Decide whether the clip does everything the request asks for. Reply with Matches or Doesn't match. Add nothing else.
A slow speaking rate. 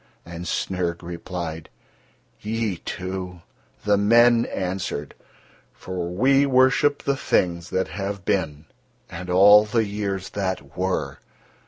Matches